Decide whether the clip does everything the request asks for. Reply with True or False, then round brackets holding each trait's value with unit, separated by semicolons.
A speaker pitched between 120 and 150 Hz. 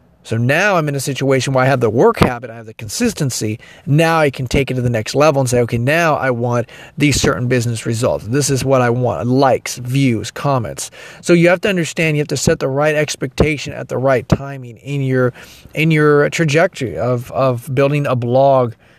True (135 Hz)